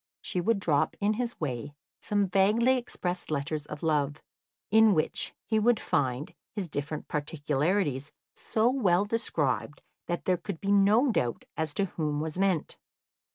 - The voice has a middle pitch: Yes, medium, 175 Hz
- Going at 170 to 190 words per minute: No, average, 155 wpm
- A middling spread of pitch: No, wide, 5.8 semitones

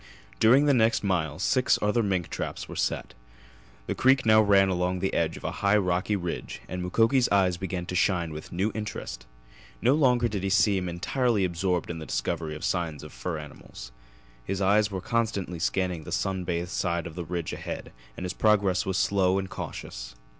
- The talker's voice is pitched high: No, very low, 95 Hz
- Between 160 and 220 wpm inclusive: Yes, average, 195 wpm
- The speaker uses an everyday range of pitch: Yes, average, 3.3 semitones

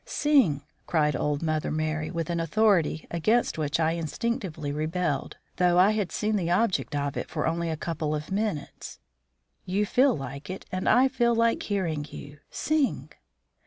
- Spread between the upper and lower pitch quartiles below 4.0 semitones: No, average, 5.3 semitones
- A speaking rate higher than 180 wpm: No, average, 165 wpm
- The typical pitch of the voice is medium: Yes, medium, 170 Hz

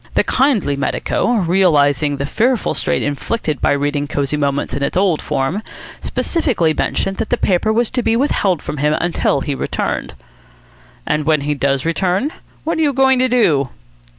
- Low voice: No, medium, 165 Hz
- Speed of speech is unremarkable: Yes, average, 175 wpm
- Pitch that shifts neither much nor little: No, wide, 8.2 semitones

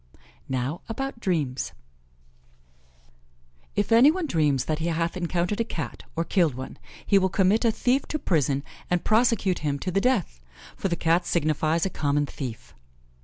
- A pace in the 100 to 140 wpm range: No, average, 165 wpm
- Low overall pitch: No, medium, 170 Hz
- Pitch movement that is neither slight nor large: No, wide, 5.7 semitones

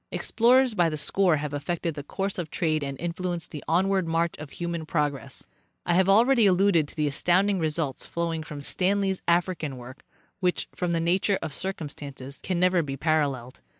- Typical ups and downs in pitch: Yes, average, 3.8 semitones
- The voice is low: No, medium, 170 Hz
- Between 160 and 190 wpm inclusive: Yes, average, 180 wpm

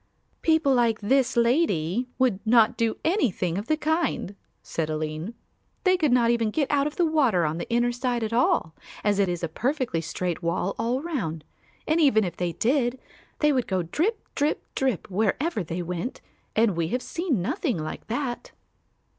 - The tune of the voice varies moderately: No, wide, 7.6 semitones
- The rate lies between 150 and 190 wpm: Yes, average, 180 wpm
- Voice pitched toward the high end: Yes, high, 235 Hz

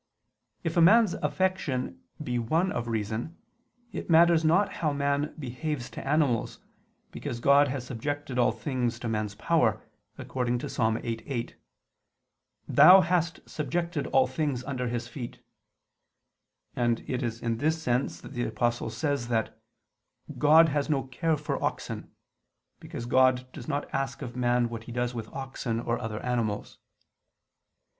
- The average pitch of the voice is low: Yes, low, 130 Hz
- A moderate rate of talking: Yes, average, 150 wpm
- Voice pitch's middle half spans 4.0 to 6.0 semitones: Yes, average, 4.3 semitones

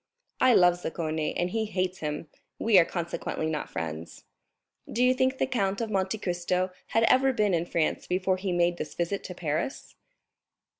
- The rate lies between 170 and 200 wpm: Yes, average, 180 wpm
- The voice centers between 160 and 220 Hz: Yes, medium, 185 Hz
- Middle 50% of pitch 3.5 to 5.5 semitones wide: Yes, average, 4.0 semitones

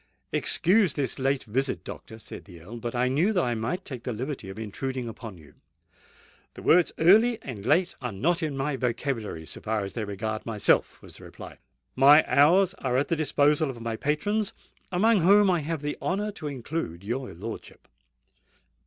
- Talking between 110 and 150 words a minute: No, average, 190 wpm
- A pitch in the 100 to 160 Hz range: Yes, low, 135 Hz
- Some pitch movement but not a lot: No, wide, 6.5 semitones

